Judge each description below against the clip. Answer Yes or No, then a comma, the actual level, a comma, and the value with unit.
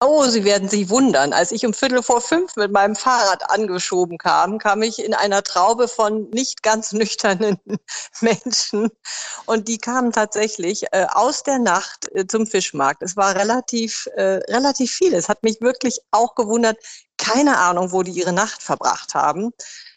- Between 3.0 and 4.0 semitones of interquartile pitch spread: Yes, average, 3.3 semitones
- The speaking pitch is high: Yes, high, 220 Hz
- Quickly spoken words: No, average, 170 wpm